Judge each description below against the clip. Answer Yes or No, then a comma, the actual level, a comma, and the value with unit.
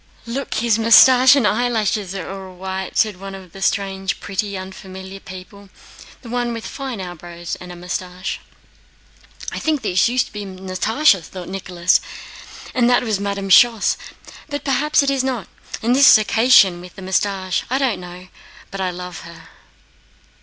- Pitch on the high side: Yes, high, 195 Hz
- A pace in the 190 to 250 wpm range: No, average, 155 wpm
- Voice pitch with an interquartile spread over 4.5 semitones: No, average, 4.2 semitones